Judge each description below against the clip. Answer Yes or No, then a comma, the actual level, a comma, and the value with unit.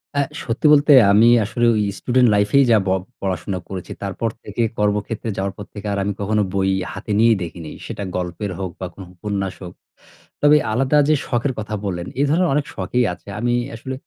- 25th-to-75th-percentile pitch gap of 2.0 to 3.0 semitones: No, average, 4.1 semitones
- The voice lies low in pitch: Yes, low, 105 Hz